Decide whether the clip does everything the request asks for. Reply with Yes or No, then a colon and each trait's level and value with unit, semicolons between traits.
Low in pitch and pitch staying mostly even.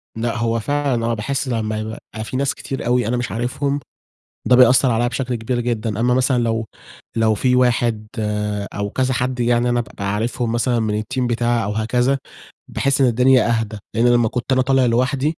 Yes: low, 120 Hz; narrow, 2.3 semitones